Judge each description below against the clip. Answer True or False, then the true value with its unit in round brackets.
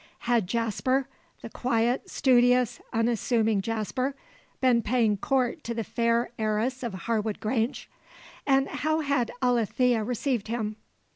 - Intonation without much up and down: True (2.3 semitones)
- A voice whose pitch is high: True (235 Hz)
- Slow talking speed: True (125 wpm)